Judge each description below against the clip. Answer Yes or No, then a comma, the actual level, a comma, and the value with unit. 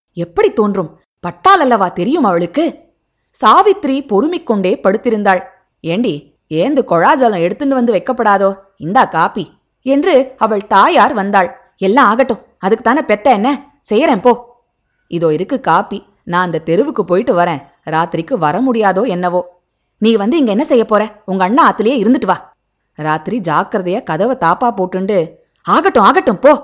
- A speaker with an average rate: No, fast, 135 wpm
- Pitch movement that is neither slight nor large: No, wide, 5.9 semitones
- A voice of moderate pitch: No, high, 210 Hz